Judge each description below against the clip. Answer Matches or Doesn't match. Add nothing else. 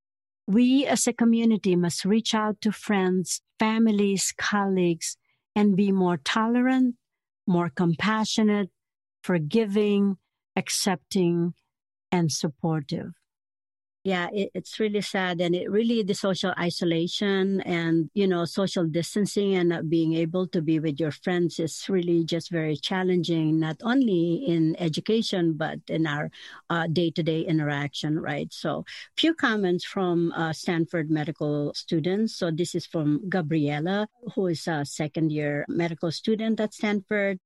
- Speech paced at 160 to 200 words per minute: Doesn't match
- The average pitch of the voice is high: Doesn't match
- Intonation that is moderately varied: Matches